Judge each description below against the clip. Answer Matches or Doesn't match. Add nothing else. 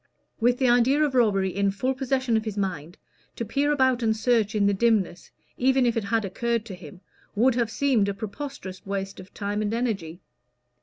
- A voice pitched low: Doesn't match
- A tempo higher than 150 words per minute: Matches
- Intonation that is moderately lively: Matches